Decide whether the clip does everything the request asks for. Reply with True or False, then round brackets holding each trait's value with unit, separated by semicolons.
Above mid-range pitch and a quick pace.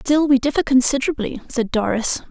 False (260 Hz; 155 wpm)